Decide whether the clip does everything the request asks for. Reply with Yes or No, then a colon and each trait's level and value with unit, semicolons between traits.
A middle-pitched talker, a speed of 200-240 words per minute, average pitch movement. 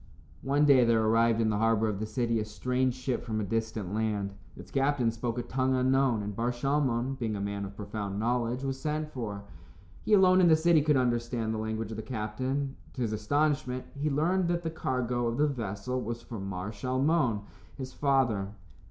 No: low, 120 Hz; fast, 205 wpm; average, 3.8 semitones